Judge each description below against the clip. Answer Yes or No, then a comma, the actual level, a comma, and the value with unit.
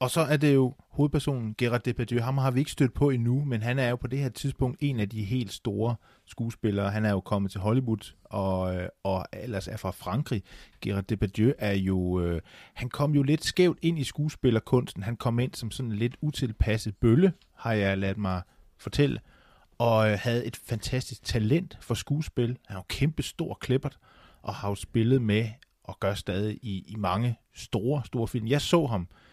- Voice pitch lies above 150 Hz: No, low, 115 Hz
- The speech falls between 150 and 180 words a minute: No, average, 200 wpm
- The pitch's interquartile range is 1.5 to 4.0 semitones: No, average, 4.4 semitones